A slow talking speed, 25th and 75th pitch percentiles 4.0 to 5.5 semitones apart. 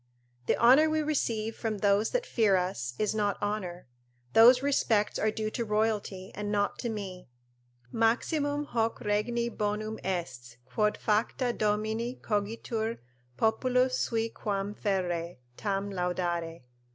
No: slow, 130 wpm; average, 2.8 semitones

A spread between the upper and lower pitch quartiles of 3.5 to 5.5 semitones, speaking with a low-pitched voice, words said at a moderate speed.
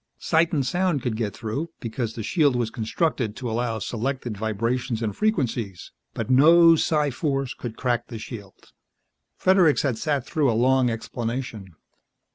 Yes: average, 4.4 semitones; low, 125 Hz; average, 155 wpm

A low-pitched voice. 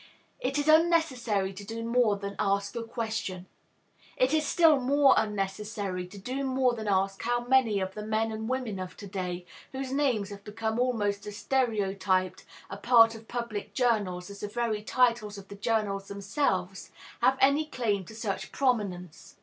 No: high, 220 Hz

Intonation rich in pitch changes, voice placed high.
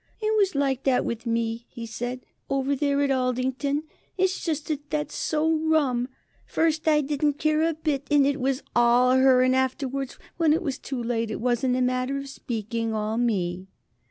No: average, 3.5 semitones; very high, 265 Hz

